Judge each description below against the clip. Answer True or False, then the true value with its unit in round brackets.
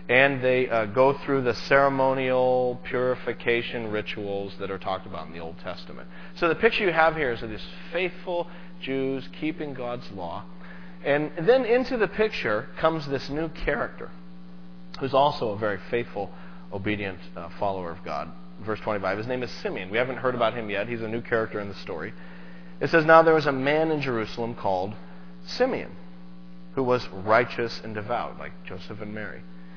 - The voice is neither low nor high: False (110 Hz)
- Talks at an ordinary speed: True (180 wpm)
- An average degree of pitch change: False (8.4 semitones)